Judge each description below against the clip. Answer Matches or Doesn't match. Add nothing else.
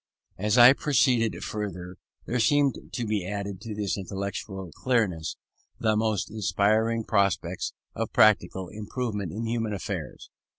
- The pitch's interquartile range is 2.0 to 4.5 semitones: Matches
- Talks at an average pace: Doesn't match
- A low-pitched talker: Matches